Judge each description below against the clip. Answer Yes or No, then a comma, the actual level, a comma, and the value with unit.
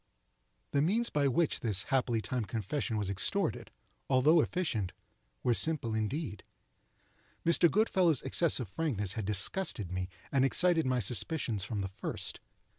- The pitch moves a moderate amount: No, wide, 7.5 semitones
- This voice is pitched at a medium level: No, low, 130 Hz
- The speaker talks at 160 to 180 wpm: No, average, 140 wpm